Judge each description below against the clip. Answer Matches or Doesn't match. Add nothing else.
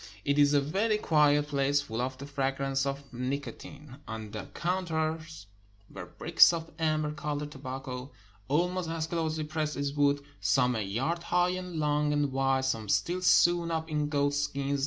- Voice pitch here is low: Doesn't match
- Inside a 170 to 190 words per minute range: Matches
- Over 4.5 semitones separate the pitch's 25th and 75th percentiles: Doesn't match